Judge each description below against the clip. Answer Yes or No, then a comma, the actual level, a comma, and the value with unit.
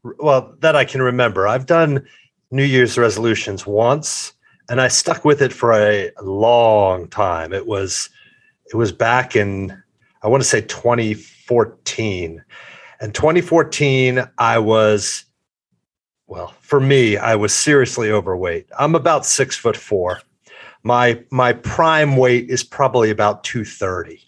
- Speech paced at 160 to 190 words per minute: No, slow, 135 wpm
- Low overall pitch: Yes, low, 120 Hz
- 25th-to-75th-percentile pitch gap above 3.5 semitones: Yes, average, 4.1 semitones